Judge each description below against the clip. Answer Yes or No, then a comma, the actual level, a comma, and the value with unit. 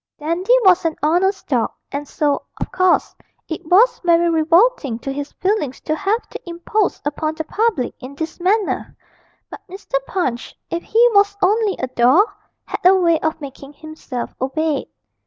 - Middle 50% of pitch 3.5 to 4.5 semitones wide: No, average, 5.0 semitones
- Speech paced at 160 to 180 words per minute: Yes, average, 165 wpm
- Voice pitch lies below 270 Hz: No, very high, 335 Hz